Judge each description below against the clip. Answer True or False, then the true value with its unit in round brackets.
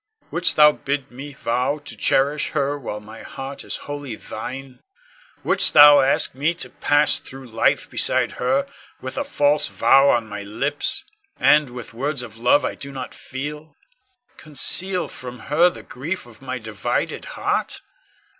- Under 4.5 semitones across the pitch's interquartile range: True (3.0 semitones)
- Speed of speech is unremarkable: True (160 wpm)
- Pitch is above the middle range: False (140 Hz)